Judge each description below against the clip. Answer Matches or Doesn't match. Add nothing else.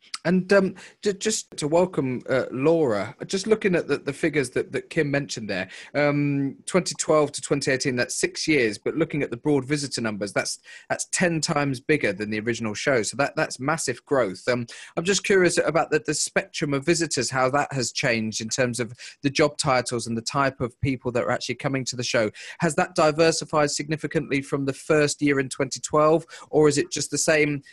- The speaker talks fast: Matches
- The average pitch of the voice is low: Doesn't match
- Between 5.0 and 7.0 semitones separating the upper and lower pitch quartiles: Doesn't match